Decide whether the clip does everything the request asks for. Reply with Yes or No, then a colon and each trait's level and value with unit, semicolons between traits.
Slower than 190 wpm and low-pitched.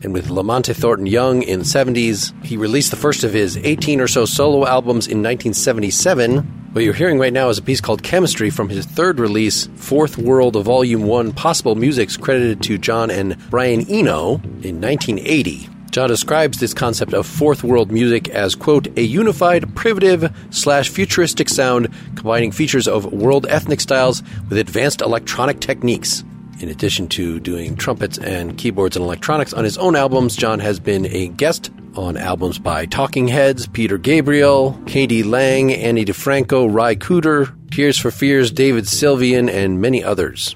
Yes: average, 165 wpm; low, 125 Hz